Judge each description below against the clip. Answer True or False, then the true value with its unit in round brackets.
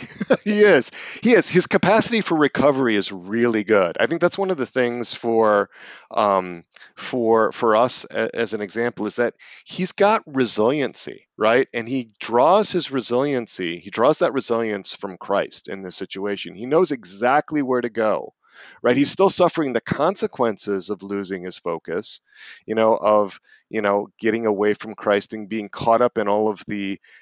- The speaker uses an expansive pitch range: True (6.3 semitones)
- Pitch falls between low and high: False (115 Hz)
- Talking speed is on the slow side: False (175 wpm)